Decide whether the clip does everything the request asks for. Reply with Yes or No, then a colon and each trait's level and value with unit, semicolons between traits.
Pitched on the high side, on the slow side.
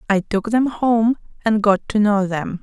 No: high, 210 Hz; fast, 205 wpm